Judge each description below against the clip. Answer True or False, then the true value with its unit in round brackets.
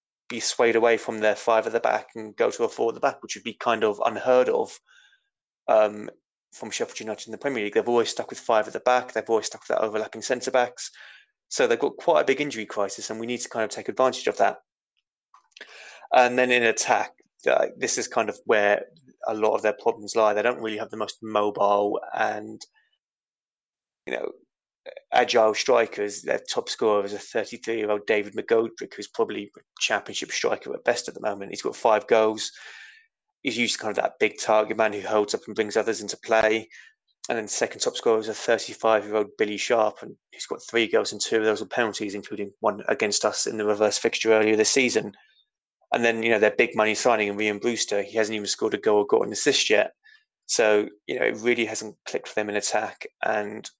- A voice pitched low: True (110 Hz)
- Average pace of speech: False (230 wpm)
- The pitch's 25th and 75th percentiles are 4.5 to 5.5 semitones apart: False (3.3 semitones)